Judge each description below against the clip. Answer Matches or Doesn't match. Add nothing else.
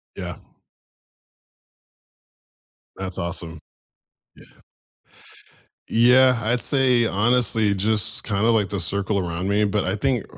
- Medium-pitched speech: Doesn't match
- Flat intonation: Doesn't match